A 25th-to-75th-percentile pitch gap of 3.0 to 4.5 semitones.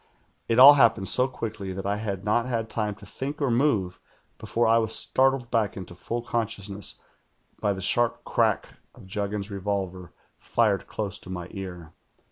Yes: average, 3.4 semitones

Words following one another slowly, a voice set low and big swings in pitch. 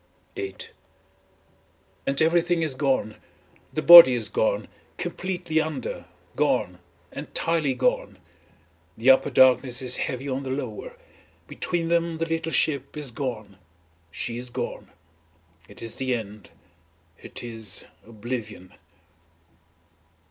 Yes: slow, 105 wpm; low, 130 Hz; wide, 6.1 semitones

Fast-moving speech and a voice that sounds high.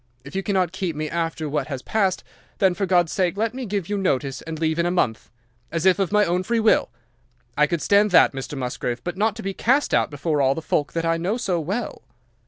No: fast, 245 wpm; medium, 175 Hz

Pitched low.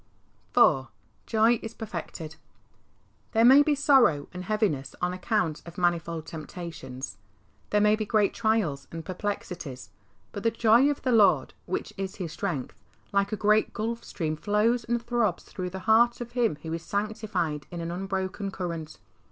No: high, 195 Hz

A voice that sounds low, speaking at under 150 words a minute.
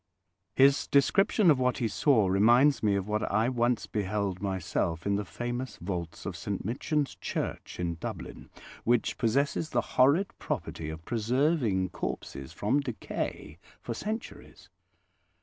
Yes: low, 115 Hz; average, 140 wpm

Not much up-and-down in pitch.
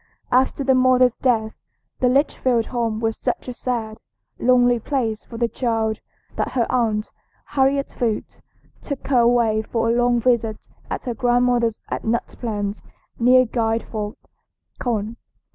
Yes: narrow, 2.1 semitones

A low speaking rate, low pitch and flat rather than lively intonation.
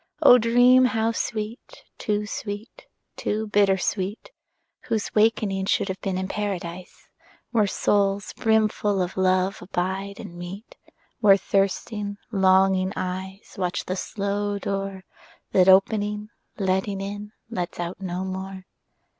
No: slow, 125 wpm; high, 195 Hz; narrow, 1.9 semitones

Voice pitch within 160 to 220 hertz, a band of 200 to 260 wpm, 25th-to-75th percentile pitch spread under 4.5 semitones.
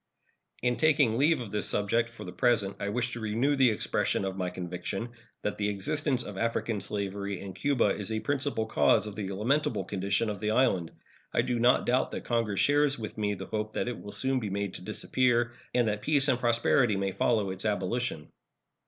No: low, 110 Hz; fast, 205 wpm; average, 3.6 semitones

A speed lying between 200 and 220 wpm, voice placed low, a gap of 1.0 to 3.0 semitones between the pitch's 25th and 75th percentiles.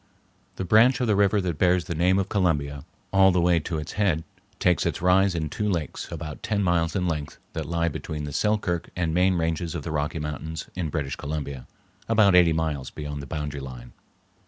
No: fast, 205 wpm; very low, 85 Hz; average, 3.6 semitones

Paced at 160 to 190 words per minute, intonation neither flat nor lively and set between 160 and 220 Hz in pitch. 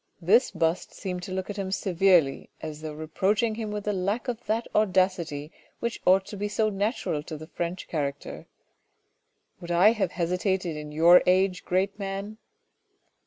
Yes: average, 175 wpm; average, 3.5 semitones; medium, 185 Hz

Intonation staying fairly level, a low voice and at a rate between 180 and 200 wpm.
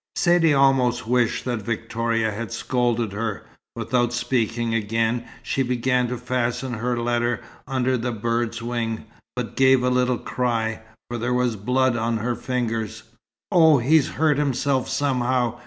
No: narrow, 1.8 semitones; low, 120 Hz; average, 145 wpm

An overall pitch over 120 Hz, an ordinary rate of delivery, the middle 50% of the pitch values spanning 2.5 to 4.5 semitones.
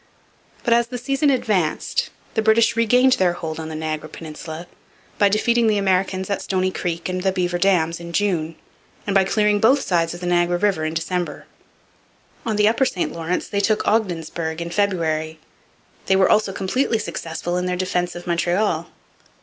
Yes: medium, 185 Hz; average, 180 wpm; average, 3.8 semitones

